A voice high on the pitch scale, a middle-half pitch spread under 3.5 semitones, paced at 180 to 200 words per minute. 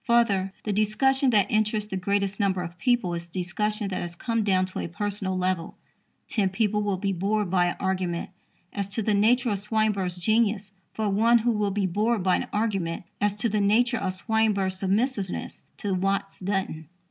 Yes: high, 200 Hz; narrow, 2.5 semitones; average, 190 wpm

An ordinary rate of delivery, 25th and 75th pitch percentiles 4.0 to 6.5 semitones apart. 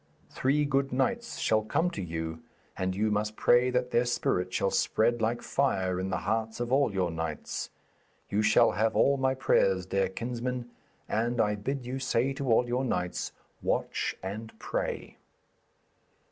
Yes: average, 165 wpm; average, 4.8 semitones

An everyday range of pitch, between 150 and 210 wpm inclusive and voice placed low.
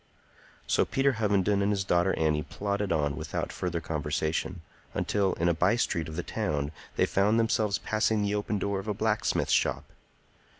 Yes: average, 4.1 semitones; average, 175 wpm; low, 100 Hz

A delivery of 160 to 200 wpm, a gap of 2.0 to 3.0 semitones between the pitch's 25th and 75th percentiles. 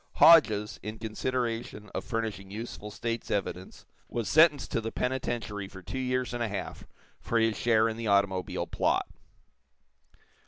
No: average, 150 wpm; average, 2.7 semitones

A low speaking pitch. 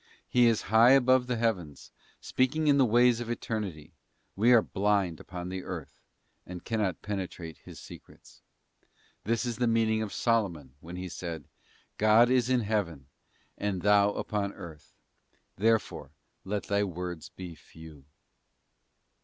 Yes: low, 105 Hz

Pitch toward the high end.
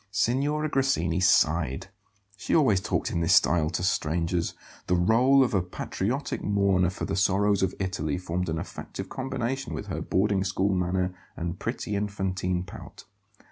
No: very low, 95 Hz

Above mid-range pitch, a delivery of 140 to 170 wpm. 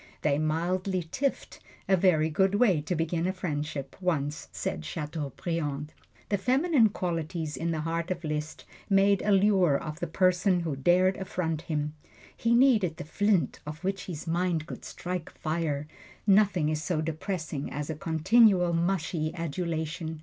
No: medium, 170 Hz; average, 150 wpm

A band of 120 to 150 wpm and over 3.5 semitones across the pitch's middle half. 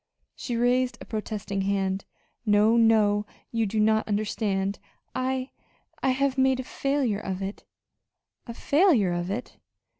Yes: average, 140 wpm; average, 4.2 semitones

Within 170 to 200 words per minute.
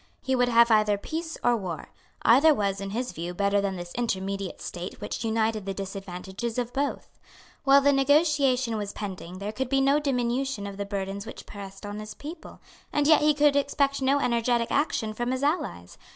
Yes: average, 195 wpm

